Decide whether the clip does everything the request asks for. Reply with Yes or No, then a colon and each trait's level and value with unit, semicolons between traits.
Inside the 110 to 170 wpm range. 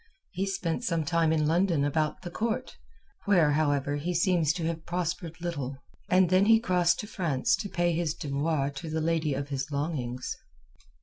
No: average, 180 wpm